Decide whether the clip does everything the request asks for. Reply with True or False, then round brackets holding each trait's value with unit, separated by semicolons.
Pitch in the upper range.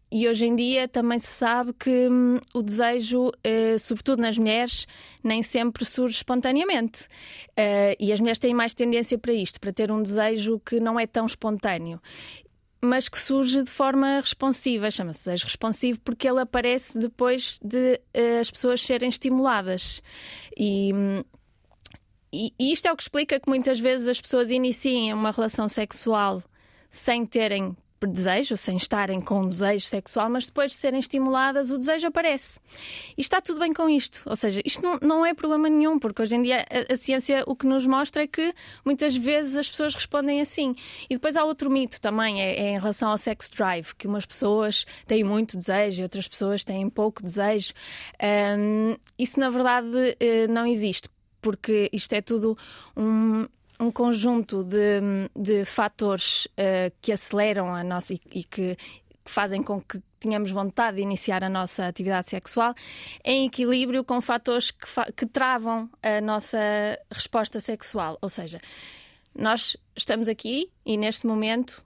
True (230 Hz)